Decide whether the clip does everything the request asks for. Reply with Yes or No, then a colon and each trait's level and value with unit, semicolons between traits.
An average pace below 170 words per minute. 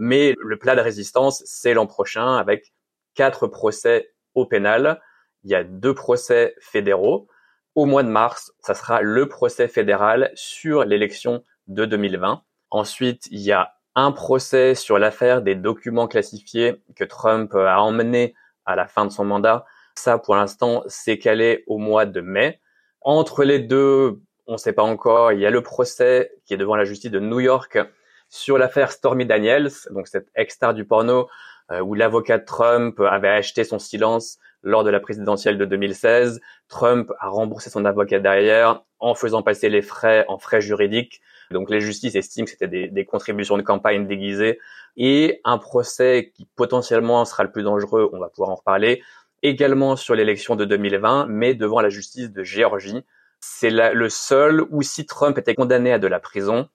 No: average, 180 wpm